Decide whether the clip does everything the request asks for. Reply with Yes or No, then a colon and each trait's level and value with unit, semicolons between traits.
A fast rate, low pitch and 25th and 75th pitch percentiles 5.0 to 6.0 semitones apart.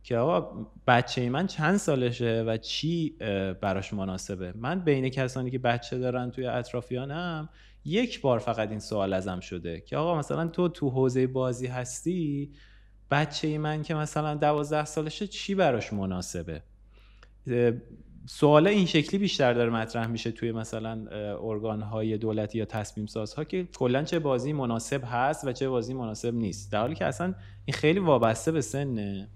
Yes: fast, 160 wpm; low, 125 Hz; wide, 5.6 semitones